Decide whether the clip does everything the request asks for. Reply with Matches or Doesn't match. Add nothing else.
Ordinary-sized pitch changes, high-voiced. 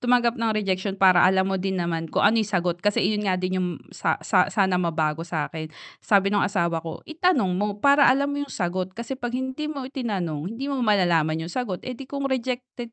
Doesn't match